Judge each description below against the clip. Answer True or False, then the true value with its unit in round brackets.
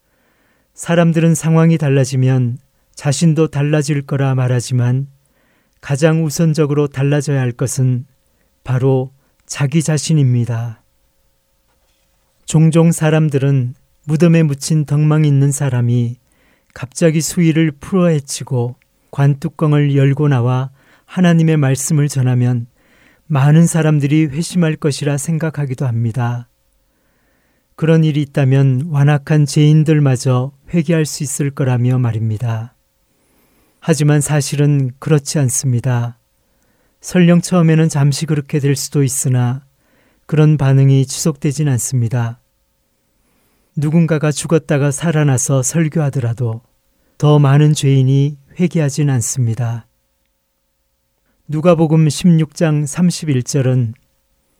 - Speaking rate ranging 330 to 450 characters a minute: False (245 characters per minute)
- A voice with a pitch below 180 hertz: True (140 Hz)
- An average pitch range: True (3.8 semitones)